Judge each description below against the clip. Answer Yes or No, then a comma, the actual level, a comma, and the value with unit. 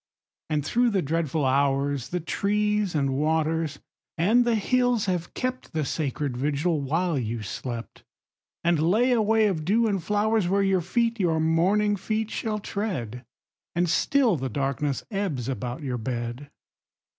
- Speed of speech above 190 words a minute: No, average, 155 wpm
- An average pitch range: No, wide, 7.0 semitones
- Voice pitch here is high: No, medium, 165 Hz